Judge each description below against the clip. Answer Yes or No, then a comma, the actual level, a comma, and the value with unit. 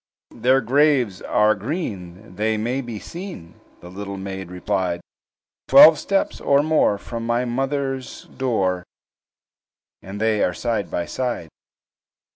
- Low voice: Yes, low, 110 Hz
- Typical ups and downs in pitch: No, wide, 5.7 semitones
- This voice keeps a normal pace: No, slow, 125 wpm